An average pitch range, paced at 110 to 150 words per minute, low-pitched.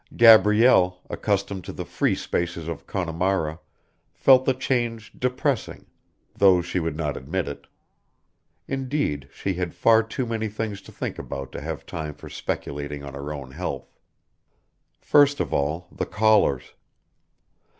No: wide, 6.8 semitones; average, 140 wpm; very low, 95 Hz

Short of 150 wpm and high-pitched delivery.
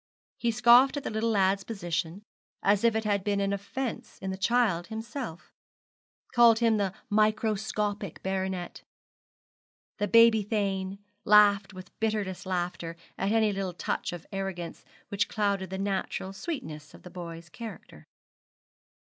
Yes: average, 140 wpm; high, 200 Hz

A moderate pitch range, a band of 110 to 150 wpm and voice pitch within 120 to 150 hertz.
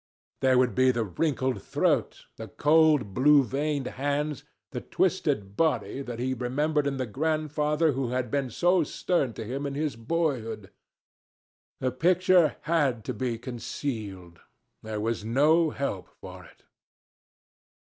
Yes: average, 4.2 semitones; average, 140 wpm; low, 135 Hz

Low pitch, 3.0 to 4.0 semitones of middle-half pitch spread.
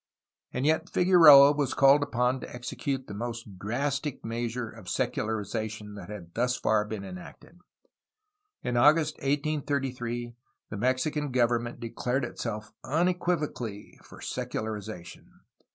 No: low, 120 Hz; average, 4.6 semitones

